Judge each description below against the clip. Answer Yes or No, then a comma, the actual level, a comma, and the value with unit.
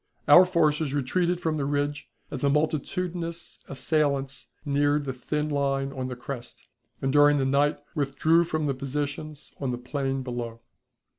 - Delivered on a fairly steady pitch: Yes, narrow, 2.1 semitones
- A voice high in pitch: No, medium, 145 Hz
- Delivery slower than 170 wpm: Yes, average, 155 wpm